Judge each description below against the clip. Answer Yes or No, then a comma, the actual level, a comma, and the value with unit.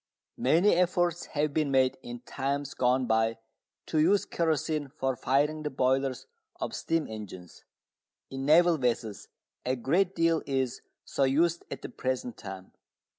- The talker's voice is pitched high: No, low, 135 Hz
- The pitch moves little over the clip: No, average, 4.1 semitones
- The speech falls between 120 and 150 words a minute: Yes, average, 145 wpm